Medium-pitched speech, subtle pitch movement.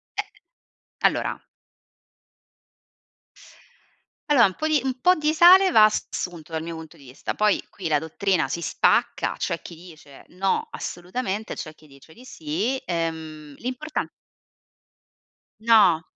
No: medium, 180 Hz; wide, 7.4 semitones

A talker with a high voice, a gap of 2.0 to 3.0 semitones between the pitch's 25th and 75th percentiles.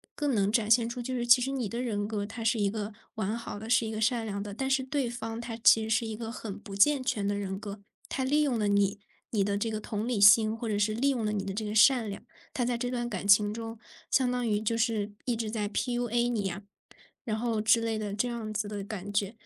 Yes: high, 220 Hz; narrow, 2.6 semitones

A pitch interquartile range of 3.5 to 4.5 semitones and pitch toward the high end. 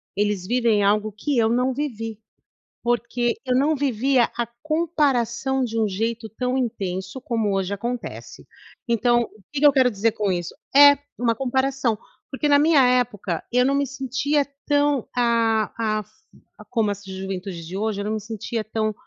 Yes: average, 3.9 semitones; high, 235 Hz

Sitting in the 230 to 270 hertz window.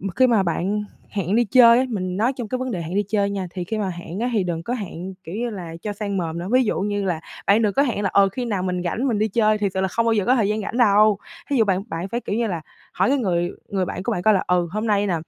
No: high, 205 Hz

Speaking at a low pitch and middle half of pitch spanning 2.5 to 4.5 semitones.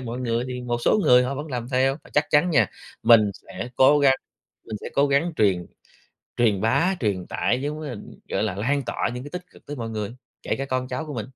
Yes: low, 125 Hz; average, 3.9 semitones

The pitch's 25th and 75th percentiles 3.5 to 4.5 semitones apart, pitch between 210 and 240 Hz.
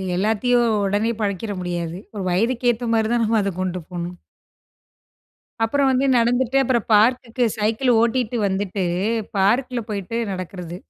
Yes: average, 4.1 semitones; high, 220 Hz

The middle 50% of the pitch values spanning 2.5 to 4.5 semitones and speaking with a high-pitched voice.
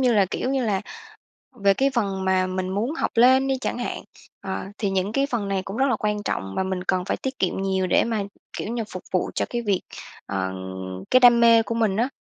Yes: average, 4.1 semitones; high, 205 Hz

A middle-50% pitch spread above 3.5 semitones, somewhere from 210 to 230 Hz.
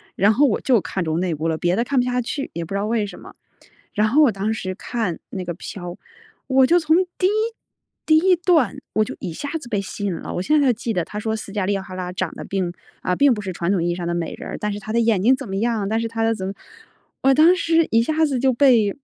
Yes: wide, 5.6 semitones; high, 220 Hz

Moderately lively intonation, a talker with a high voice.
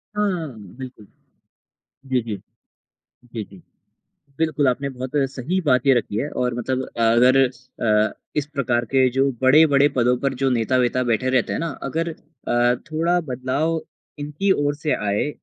No: average, 3.2 semitones; low, 130 Hz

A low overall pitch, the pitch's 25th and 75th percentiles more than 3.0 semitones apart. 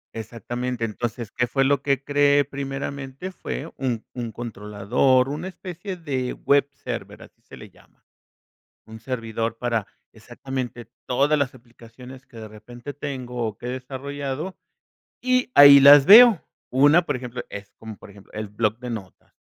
Yes: low, 130 Hz; average, 3.5 semitones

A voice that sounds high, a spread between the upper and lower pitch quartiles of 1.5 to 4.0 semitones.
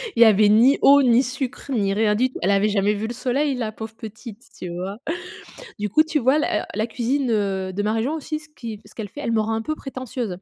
Yes: high, 225 Hz; average, 3.7 semitones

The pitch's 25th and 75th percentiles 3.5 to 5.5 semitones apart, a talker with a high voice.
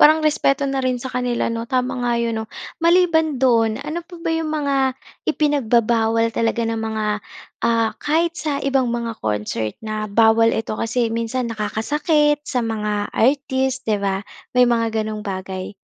Yes: average, 4.1 semitones; high, 235 Hz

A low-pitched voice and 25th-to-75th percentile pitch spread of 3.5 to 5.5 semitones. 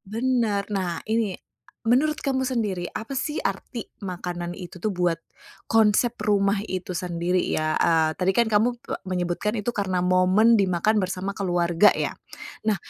No: high, 195 Hz; average, 3.8 semitones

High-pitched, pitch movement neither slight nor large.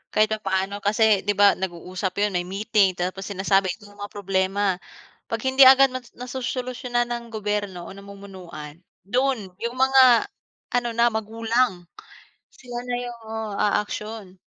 Yes: high, 210 Hz; average, 3.8 semitones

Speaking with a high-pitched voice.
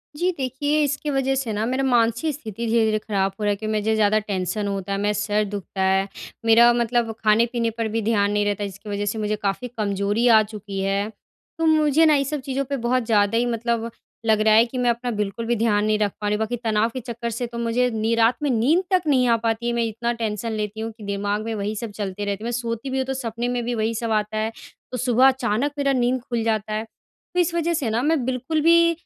Yes: high, 230 Hz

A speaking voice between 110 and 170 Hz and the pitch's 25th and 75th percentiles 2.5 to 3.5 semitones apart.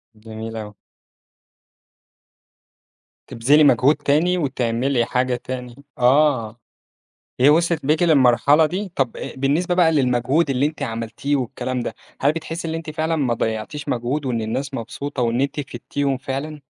No: low, 135 Hz; average, 4.0 semitones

